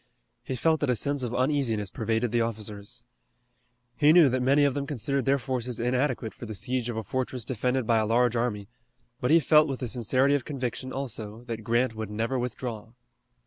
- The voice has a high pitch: No, low, 125 Hz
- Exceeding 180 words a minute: Yes, average, 200 wpm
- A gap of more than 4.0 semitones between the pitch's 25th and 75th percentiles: No, average, 3.0 semitones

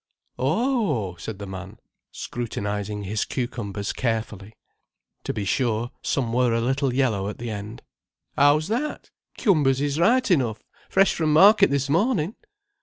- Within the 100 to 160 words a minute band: Yes, average, 140 wpm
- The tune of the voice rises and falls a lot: Yes, wide, 6.4 semitones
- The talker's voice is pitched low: Yes, low, 125 Hz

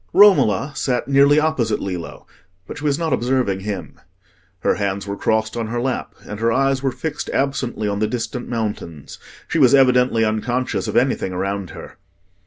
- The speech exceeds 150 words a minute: Yes, average, 175 wpm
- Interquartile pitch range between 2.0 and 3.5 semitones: No, average, 4.6 semitones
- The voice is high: No, low, 120 Hz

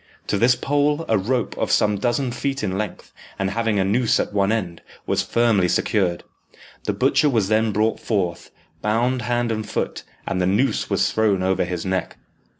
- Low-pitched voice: Yes, low, 110 Hz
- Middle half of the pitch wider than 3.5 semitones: Yes, average, 3.9 semitones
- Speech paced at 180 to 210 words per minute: Yes, average, 185 wpm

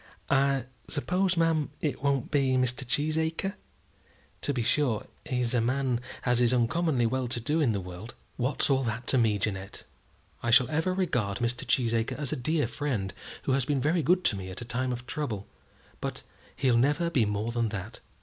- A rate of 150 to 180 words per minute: No, average, 190 wpm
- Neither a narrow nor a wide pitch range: Yes, average, 4.0 semitones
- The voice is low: Yes, low, 125 Hz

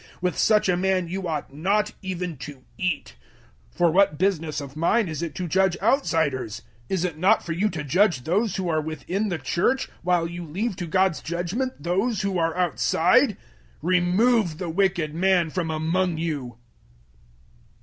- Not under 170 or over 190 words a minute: Yes, average, 175 wpm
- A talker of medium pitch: Yes, medium, 175 Hz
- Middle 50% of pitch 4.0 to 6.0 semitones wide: No, average, 3.2 semitones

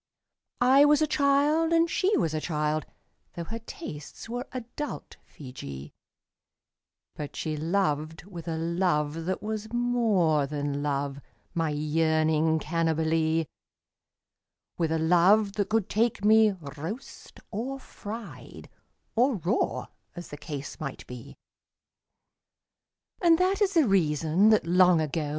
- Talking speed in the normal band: No, slow, 130 wpm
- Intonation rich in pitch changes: Yes, wide, 6.7 semitones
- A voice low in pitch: No, medium, 170 Hz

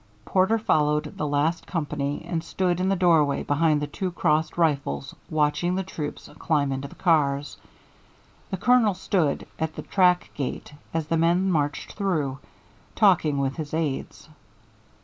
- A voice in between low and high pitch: Yes, medium, 160 Hz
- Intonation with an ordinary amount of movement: Yes, average, 3.6 semitones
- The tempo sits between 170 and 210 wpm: No, average, 150 wpm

